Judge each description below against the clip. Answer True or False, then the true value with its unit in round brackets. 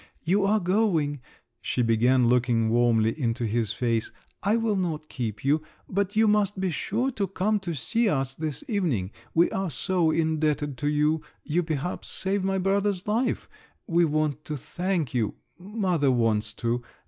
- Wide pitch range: True (7.6 semitones)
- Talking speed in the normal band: True (160 wpm)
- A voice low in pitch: False (160 Hz)